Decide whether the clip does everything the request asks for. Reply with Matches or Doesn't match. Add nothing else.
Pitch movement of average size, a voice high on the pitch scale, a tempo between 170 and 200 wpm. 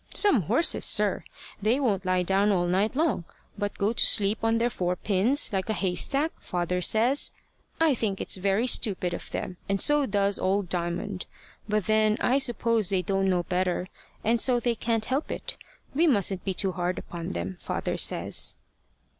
Matches